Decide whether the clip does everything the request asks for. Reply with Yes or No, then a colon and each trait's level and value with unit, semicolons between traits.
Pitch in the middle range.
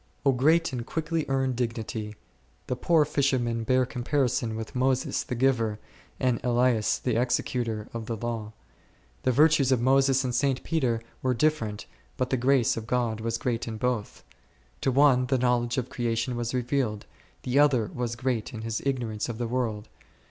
No: low, 125 Hz